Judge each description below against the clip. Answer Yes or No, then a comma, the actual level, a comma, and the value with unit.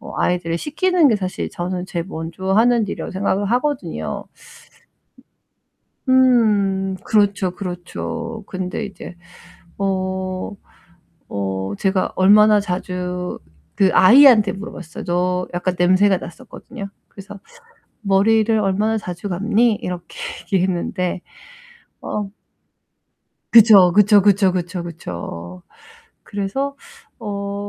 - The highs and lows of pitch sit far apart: No, average, 2.8 semitones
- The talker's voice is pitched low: No, high, 195 Hz